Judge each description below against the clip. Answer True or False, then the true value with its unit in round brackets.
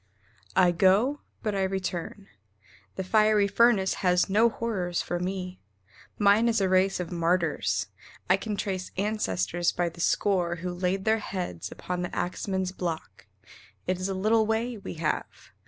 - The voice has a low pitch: False (190 Hz)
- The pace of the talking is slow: False (155 wpm)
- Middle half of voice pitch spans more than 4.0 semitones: False (2.9 semitones)